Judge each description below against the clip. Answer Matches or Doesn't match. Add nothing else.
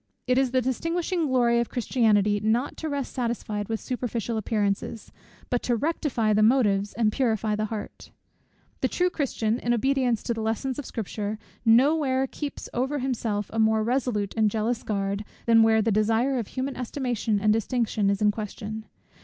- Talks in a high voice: Matches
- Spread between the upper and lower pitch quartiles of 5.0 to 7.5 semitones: Doesn't match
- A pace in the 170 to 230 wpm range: Matches